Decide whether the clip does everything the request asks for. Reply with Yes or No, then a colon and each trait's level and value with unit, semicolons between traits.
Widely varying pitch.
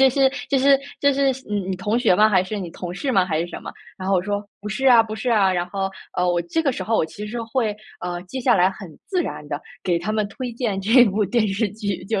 No: average, 4.5 semitones